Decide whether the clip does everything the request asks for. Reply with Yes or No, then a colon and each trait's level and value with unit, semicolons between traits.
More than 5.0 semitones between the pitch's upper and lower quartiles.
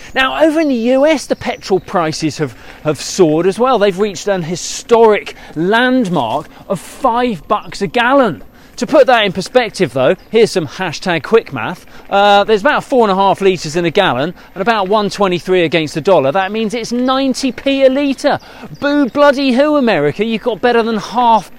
Yes: wide, 5.4 semitones